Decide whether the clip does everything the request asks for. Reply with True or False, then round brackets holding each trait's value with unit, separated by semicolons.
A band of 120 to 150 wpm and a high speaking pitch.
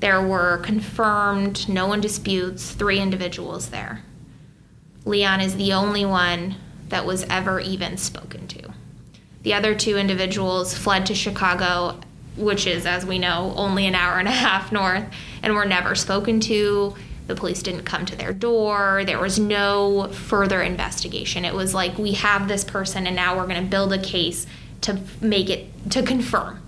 False (170 wpm; 195 Hz)